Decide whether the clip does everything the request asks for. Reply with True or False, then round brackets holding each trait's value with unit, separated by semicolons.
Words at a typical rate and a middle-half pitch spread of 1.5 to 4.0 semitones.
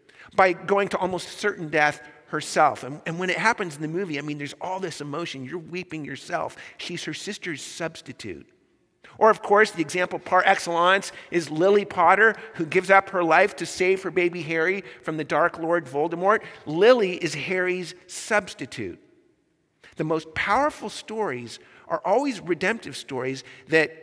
True (165 wpm; 3.6 semitones)